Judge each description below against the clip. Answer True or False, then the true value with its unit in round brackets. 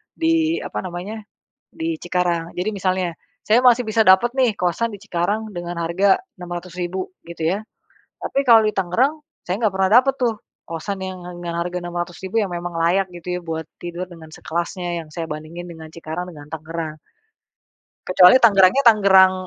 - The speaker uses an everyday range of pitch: True (3.1 semitones)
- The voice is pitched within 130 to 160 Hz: False (180 Hz)